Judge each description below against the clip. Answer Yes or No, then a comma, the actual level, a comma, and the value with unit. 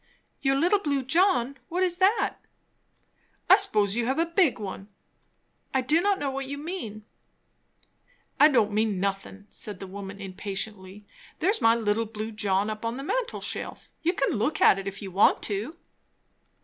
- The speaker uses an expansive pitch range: Yes, wide, 7.1 semitones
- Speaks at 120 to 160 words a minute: No, average, 175 wpm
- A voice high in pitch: Yes, high, 230 Hz